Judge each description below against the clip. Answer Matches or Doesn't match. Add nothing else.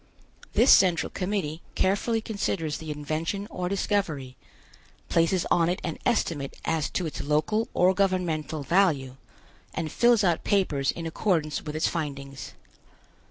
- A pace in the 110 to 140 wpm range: Matches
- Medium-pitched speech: Matches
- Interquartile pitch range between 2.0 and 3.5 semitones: Doesn't match